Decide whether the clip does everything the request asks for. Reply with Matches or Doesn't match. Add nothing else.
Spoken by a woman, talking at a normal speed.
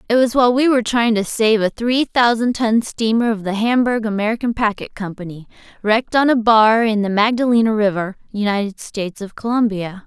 Matches